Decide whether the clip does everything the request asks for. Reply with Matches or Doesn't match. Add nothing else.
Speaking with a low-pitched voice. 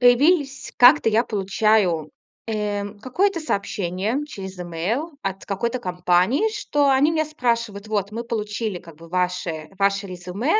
Doesn't match